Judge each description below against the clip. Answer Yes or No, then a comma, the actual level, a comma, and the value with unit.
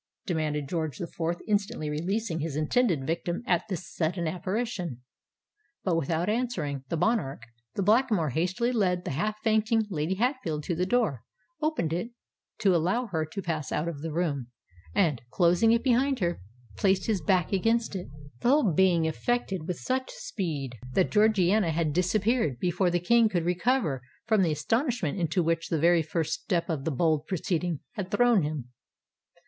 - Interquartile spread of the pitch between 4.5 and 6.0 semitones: Yes, wide, 5.4 semitones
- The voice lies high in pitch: No, medium, 175 Hz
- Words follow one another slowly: No, average, 165 wpm